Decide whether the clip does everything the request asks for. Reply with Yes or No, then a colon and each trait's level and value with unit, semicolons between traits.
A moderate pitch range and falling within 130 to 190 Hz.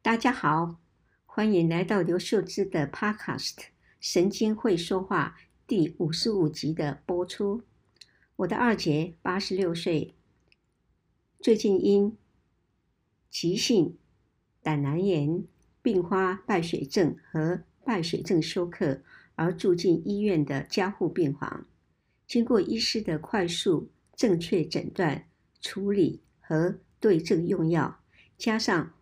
Yes: average, 3.4 semitones; medium, 185 Hz